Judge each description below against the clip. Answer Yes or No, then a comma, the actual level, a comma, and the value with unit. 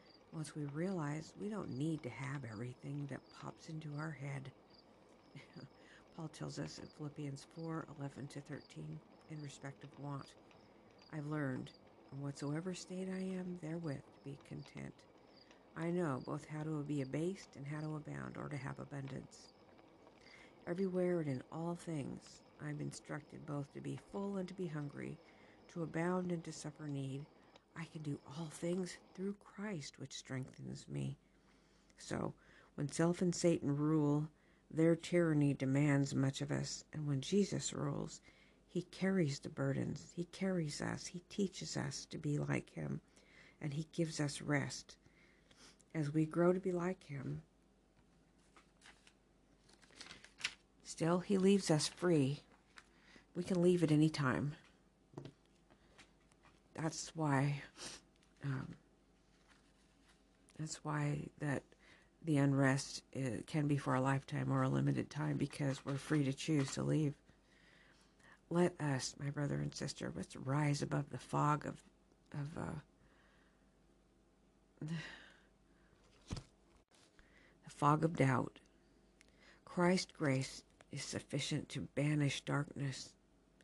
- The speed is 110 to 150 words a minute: Yes, slow, 135 wpm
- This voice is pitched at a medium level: Yes, medium, 150 Hz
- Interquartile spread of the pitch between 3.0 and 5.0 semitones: Yes, average, 3.3 semitones